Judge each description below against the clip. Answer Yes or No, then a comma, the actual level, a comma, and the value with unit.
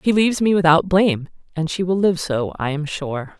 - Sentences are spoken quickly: Yes, fast, 230 wpm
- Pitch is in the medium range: Yes, medium, 170 Hz